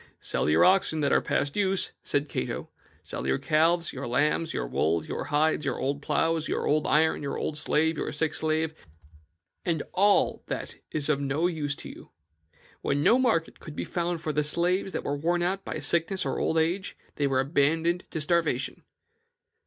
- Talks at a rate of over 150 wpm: Yes, average, 190 wpm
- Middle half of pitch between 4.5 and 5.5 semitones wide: No, average, 3.1 semitones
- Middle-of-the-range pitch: Yes, medium, 155 Hz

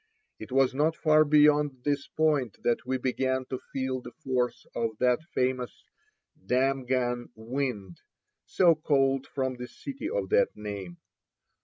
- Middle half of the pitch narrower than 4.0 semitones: Yes, average, 3.0 semitones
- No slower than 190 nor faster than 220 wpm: No, average, 140 wpm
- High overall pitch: No, low, 130 Hz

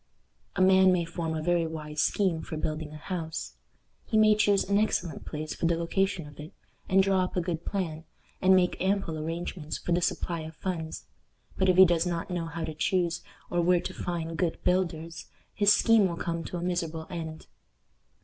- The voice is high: No, medium, 170 Hz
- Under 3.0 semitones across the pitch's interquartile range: Yes, narrow, 2.5 semitones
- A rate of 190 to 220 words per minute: Yes, average, 200 wpm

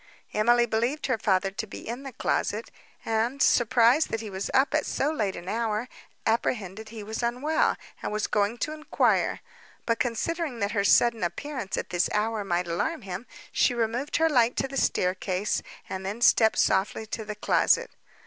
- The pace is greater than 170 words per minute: Yes, average, 180 wpm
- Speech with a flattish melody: No, average, 3.4 semitones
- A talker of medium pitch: No, high, 225 Hz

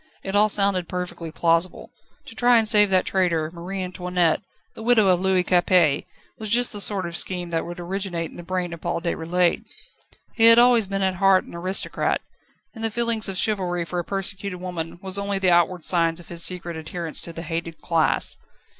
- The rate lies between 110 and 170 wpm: No, average, 200 wpm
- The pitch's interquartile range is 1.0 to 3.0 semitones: Yes, narrow, 2.6 semitones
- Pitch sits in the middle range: Yes, medium, 180 Hz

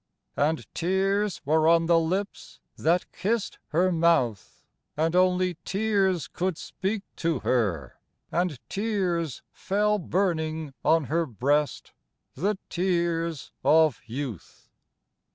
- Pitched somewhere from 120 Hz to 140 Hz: No, medium, 170 Hz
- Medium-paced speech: No, slow, 110 wpm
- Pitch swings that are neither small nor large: Yes, average, 3.2 semitones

